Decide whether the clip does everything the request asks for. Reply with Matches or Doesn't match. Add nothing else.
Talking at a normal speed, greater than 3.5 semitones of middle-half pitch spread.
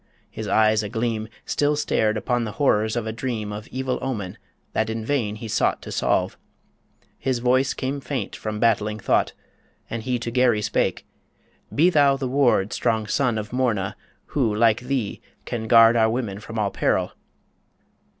Doesn't match